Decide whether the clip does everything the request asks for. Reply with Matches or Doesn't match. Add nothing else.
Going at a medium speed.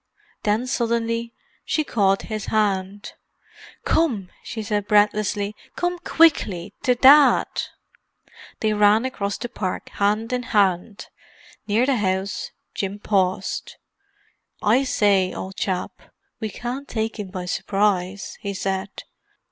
Doesn't match